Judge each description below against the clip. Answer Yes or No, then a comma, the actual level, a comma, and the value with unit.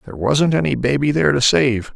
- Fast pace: Yes, fast, 215 wpm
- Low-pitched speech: Yes, low, 130 Hz